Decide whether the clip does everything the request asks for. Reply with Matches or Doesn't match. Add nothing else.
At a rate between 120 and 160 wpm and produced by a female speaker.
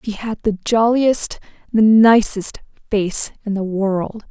Matches